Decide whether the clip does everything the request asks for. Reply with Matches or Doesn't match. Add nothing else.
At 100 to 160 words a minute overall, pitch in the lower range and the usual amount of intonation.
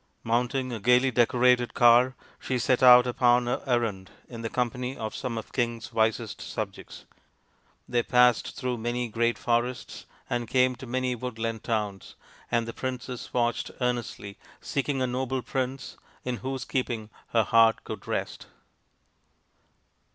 Doesn't match